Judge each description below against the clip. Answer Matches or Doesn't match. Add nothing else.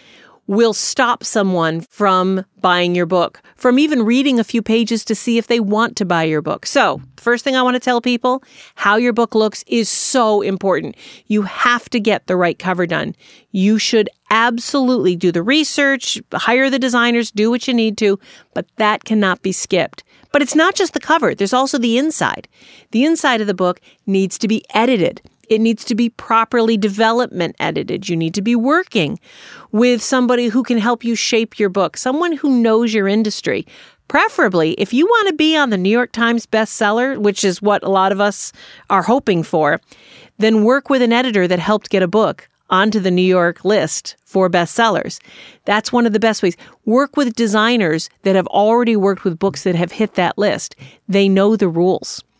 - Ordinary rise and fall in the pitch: Matches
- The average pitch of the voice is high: Matches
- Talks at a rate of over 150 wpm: Matches